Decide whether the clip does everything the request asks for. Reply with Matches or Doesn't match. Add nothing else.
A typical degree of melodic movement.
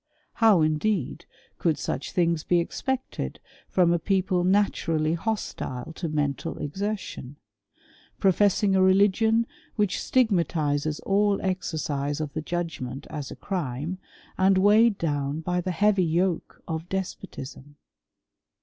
Matches